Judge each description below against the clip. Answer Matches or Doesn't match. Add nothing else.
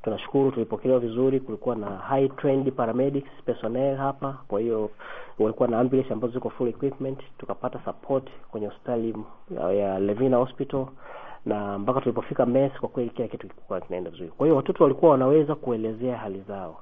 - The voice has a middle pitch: Doesn't match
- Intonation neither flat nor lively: Matches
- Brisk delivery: Matches